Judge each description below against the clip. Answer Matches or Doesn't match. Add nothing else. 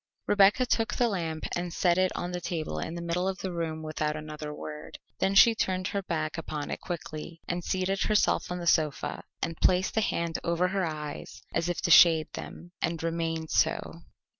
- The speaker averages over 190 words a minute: Matches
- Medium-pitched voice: Matches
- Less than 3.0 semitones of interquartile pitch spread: Matches